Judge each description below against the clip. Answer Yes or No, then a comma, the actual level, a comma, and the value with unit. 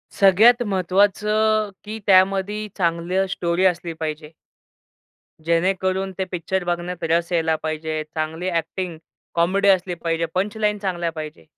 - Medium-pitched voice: Yes, medium, 180 Hz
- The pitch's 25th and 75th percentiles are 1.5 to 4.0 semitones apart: Yes, average, 2.8 semitones